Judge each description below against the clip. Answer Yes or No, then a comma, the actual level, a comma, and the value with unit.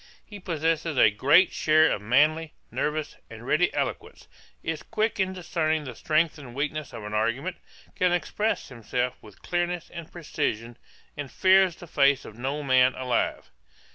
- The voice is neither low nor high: Yes, medium, 155 Hz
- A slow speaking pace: No, average, 160 wpm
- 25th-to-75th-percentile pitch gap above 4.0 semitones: Yes, average, 5.1 semitones